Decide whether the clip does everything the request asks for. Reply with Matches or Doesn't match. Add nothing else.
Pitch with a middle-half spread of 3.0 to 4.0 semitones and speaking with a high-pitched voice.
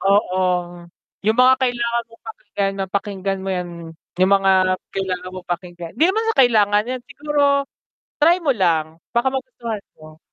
Doesn't match